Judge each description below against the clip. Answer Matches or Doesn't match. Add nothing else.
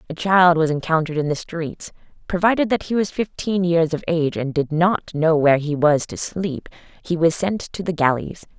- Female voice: Matches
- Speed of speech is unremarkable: Doesn't match